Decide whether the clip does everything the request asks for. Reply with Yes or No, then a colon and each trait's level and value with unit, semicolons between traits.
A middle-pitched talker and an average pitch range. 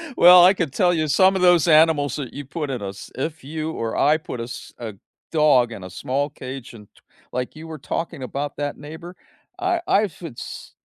Yes: medium, 150 Hz; average, 4.4 semitones